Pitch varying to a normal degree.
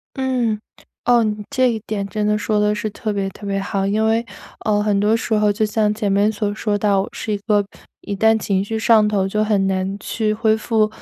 No: narrow, 1.4 semitones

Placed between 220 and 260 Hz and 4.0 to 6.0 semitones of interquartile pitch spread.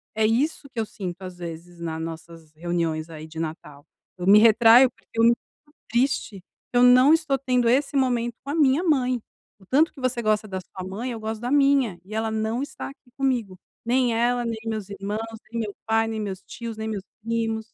Yes: high, 225 Hz; average, 4.7 semitones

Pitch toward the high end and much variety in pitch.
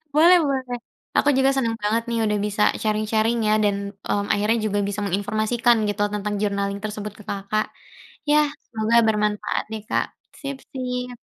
No: high, 215 Hz; narrow, 2.6 semitones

